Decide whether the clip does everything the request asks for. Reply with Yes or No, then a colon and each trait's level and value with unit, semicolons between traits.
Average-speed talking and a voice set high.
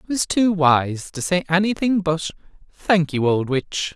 No: average, 180 wpm; medium, 170 Hz